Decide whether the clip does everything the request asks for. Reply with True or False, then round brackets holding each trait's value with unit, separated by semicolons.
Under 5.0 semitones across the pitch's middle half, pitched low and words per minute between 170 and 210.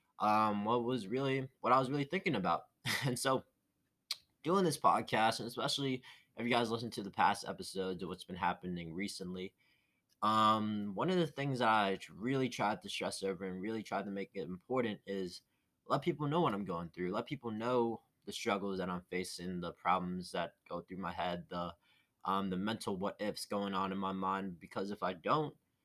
False (5.4 semitones; 110 Hz; 200 wpm)